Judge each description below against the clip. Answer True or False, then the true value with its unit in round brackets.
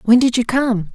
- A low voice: False (235 Hz)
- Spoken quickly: True (255 wpm)